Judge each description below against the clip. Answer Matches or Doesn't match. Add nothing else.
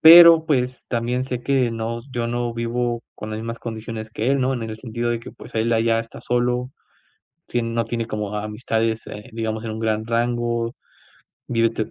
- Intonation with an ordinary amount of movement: Doesn't match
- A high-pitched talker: Doesn't match